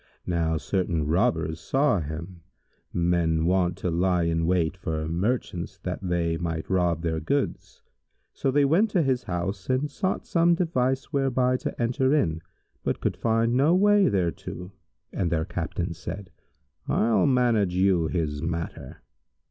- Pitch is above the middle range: No, very low, 90 Hz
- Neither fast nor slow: Yes, average, 150 wpm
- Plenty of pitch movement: Yes, wide, 7.3 semitones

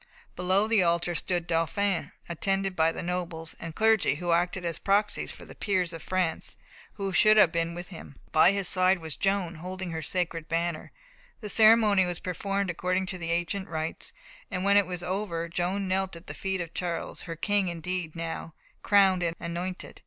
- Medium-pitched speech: Yes, medium, 180 Hz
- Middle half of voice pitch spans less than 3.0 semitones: Yes, narrow, 2.5 semitones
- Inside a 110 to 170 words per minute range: No, average, 190 wpm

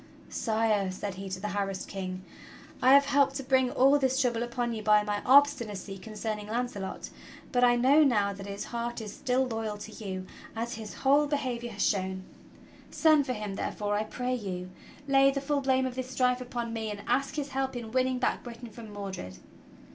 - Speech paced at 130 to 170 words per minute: No, fast, 205 wpm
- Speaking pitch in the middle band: No, high, 235 Hz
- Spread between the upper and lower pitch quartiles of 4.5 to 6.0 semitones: No, average, 4.0 semitones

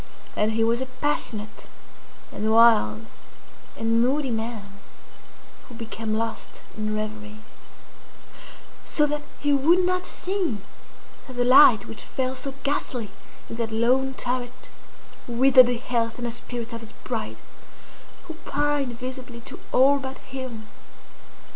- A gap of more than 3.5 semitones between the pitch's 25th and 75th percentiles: No, average, 3.0 semitones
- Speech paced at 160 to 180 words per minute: No, slow, 135 wpm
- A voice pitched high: Yes, high, 245 Hz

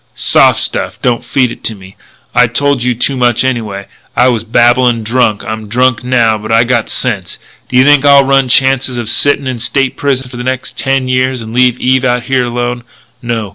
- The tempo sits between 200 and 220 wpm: Yes, fast, 205 wpm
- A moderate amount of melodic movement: No, narrow, 1.8 semitones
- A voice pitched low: Yes, low, 125 Hz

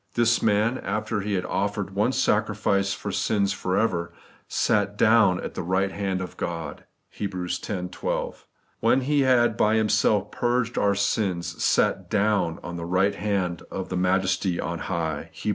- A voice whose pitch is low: Yes, low, 100 Hz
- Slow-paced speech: No, average, 175 wpm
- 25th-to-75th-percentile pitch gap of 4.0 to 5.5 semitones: No, average, 3.1 semitones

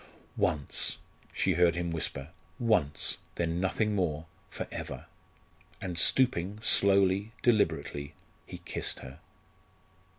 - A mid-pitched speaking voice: No, very low, 90 Hz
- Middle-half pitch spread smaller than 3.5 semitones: No, average, 4.2 semitones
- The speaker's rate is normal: No, slow, 105 wpm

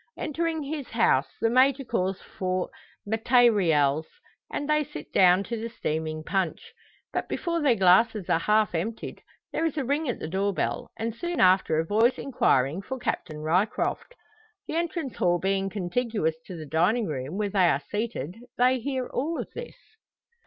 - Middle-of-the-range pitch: No, high, 210 Hz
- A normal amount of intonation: No, wide, 6.7 semitones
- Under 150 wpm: No, average, 165 wpm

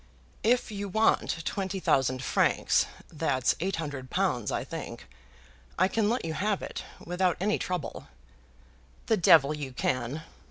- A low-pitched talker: No, medium, 170 Hz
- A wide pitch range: Yes, wide, 5.9 semitones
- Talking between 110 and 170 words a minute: Yes, average, 145 wpm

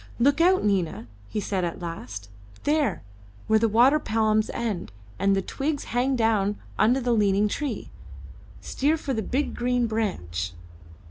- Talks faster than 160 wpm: No, average, 150 wpm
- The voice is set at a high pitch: Yes, high, 220 Hz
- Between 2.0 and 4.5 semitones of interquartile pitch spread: No, average, 5.0 semitones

